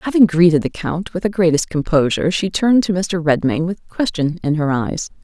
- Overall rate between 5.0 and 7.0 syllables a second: Yes, 5.4 syllables/s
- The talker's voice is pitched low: No, medium, 170 Hz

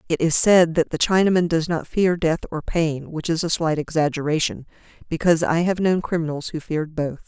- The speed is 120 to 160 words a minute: No, fast, 205 wpm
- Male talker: No, female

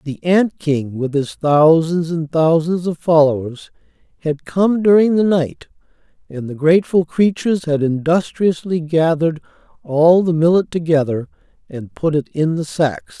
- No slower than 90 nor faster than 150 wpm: Yes, average, 145 wpm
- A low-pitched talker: No, medium, 160 Hz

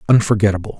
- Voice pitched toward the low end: Yes, low, 105 Hz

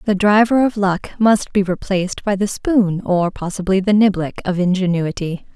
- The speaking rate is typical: Yes, average, 150 wpm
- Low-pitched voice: No, high, 195 Hz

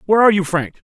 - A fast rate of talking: Yes, fast, 260 wpm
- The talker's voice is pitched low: No, high, 190 Hz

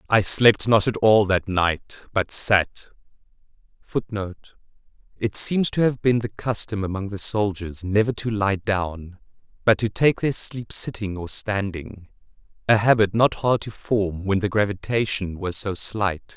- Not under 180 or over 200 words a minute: No, average, 160 wpm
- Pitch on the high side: No, low, 105 Hz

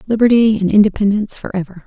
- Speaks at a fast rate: No, average, 160 wpm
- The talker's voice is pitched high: Yes, high, 205 Hz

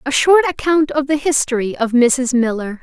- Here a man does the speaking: No, female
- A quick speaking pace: No, average, 190 wpm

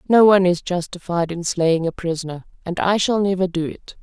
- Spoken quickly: Yes, fast, 210 wpm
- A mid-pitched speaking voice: Yes, medium, 180 Hz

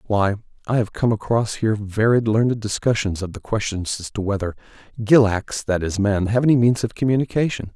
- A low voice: Yes, low, 110 Hz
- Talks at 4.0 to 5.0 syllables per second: No, 5.6 syllables/s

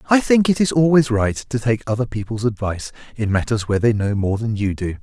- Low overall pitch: Yes, low, 115 Hz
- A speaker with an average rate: No, fast, 240 wpm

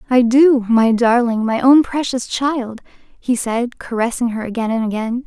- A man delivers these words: No, female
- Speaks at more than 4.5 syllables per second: Yes, 4.7 syllables/s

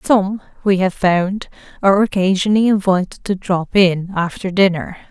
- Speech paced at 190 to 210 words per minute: No, average, 140 wpm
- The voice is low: No, high, 190 Hz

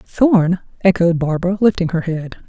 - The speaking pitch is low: No, medium, 180 Hz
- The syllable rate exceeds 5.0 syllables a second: No, 4.9 syllables/s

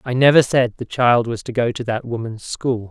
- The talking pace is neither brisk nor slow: No, fast, 250 wpm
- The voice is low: Yes, low, 120 Hz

